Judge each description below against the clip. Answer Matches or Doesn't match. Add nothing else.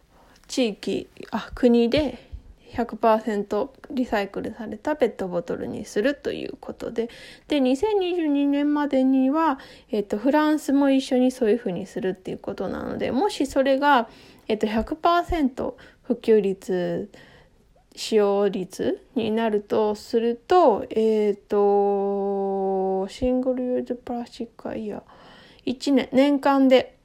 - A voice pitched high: Matches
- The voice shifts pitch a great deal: Doesn't match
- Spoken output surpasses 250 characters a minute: Doesn't match